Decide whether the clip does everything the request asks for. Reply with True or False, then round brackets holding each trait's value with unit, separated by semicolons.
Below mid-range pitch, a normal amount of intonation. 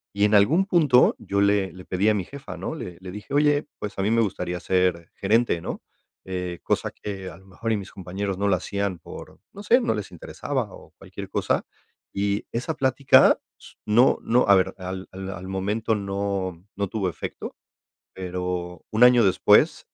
True (100 Hz; 3.3 semitones)